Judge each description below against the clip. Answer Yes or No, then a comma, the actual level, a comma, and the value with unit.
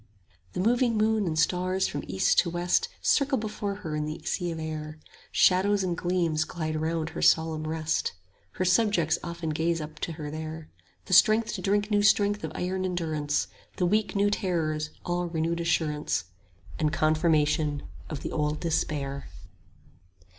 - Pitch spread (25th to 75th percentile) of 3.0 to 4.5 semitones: Yes, average, 3.3 semitones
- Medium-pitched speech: Yes, medium, 165 Hz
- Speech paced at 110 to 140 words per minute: No, average, 165 wpm